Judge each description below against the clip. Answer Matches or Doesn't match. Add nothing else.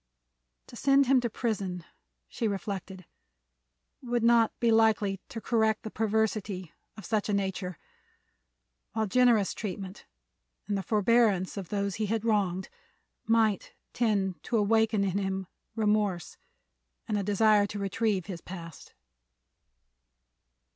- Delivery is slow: Matches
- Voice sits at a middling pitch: Doesn't match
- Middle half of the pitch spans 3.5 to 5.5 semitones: Doesn't match